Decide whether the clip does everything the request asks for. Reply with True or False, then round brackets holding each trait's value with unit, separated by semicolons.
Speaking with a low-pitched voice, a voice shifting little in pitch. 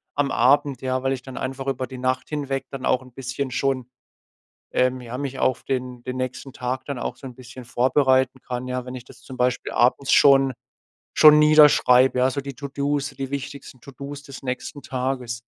True (130 Hz; 1.4 semitones)